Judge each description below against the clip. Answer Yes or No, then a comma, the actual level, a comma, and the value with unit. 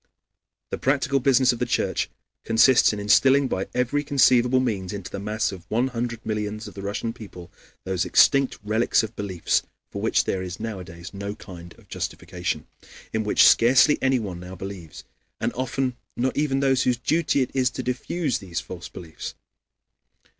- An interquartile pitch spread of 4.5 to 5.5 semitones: Yes, average, 4.9 semitones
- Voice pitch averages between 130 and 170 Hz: No, low, 115 Hz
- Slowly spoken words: No, average, 170 wpm